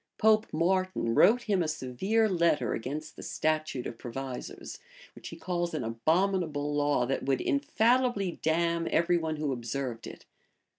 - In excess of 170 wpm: No, average, 150 wpm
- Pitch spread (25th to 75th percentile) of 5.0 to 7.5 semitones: Yes, wide, 5.5 semitones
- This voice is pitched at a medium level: Yes, medium, 155 Hz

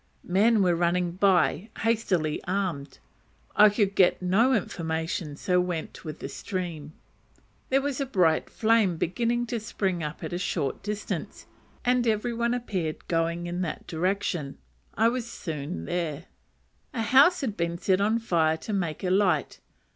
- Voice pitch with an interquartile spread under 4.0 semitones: No, average, 5.1 semitones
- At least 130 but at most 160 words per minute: Yes, average, 155 wpm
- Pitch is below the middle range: No, medium, 185 Hz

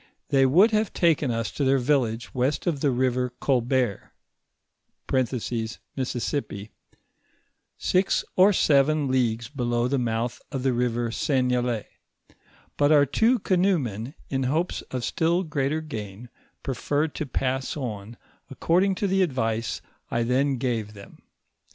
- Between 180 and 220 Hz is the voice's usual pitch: No, low, 130 Hz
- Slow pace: Yes, slow, 130 wpm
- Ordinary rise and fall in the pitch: Yes, average, 4.0 semitones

